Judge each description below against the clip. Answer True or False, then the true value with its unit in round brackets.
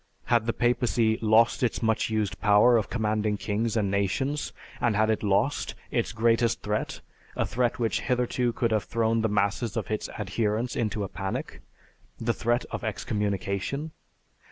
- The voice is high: False (110 Hz)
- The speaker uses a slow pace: False (160 wpm)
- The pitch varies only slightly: True (2.2 semitones)